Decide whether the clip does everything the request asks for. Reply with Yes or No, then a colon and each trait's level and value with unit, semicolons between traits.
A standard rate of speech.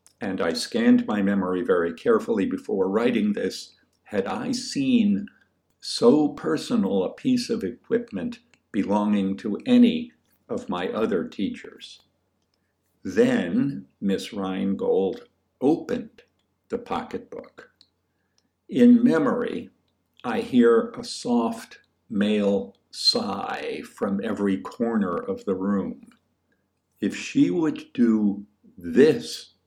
No: slow, 105 wpm